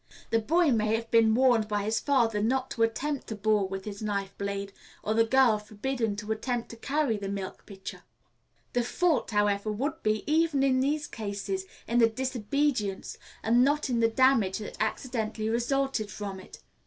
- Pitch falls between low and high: No, high, 225 Hz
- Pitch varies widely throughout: No, average, 4.0 semitones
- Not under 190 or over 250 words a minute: No, average, 180 wpm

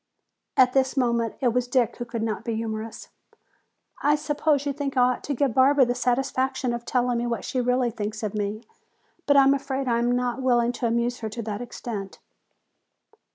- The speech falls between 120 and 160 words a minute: No, average, 200 wpm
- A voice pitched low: No, high, 245 Hz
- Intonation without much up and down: Yes, narrow, 2.2 semitones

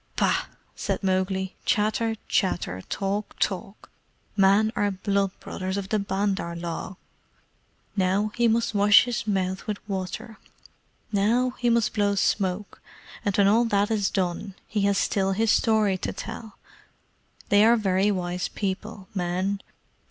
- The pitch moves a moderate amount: No, narrow, 2.1 semitones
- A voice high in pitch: Yes, high, 200 Hz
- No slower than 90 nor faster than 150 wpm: Yes, average, 140 wpm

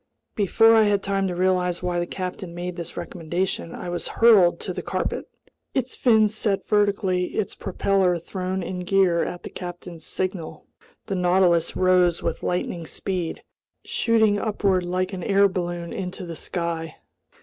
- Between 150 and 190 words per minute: Yes, average, 160 wpm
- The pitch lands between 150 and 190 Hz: Yes, medium, 185 Hz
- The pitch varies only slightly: Yes, narrow, 2.1 semitones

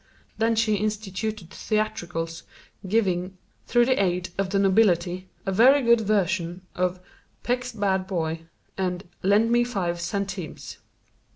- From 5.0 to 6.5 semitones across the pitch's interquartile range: No, average, 3.5 semitones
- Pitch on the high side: Yes, high, 195 Hz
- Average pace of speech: No, slow, 125 wpm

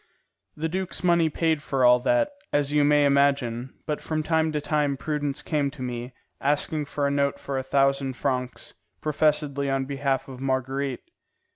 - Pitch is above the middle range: No, medium, 140 Hz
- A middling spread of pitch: No, narrow, 2.0 semitones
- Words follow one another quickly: No, average, 170 wpm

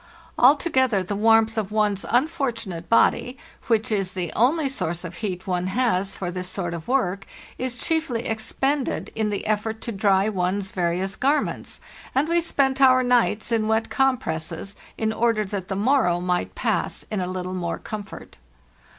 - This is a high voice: Yes, high, 215 Hz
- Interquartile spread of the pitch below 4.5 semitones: No, average, 5.1 semitones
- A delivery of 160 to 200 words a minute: Yes, average, 170 wpm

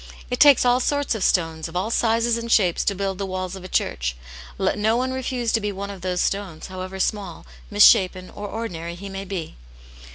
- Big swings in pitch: No, average, 3.7 semitones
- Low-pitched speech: No, high, 195 Hz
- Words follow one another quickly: Yes, fast, 220 wpm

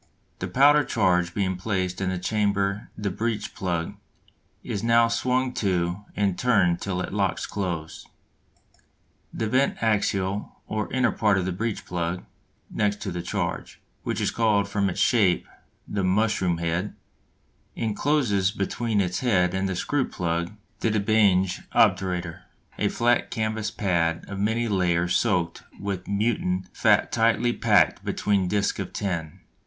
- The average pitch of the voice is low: Yes, low, 100 Hz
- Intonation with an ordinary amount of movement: Yes, average, 3.3 semitones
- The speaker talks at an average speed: Yes, average, 150 wpm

